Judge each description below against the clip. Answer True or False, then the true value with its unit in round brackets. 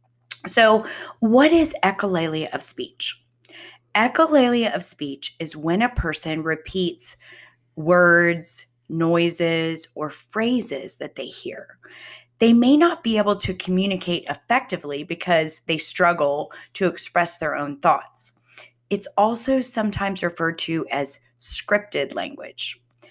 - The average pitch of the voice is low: False (170 Hz)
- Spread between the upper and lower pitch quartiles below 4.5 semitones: False (5.1 semitones)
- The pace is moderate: False (115 wpm)